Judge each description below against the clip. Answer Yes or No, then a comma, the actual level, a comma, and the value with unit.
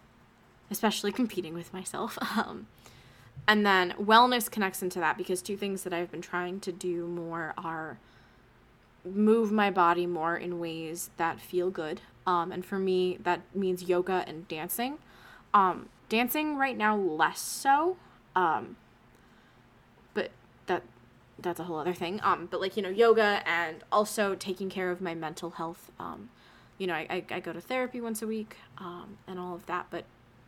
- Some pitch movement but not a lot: Yes, average, 3.3 semitones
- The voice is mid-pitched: Yes, medium, 180 Hz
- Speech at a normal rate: Yes, average, 170 wpm